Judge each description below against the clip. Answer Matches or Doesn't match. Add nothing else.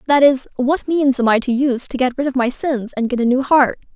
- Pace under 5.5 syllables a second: Doesn't match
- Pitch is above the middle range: Matches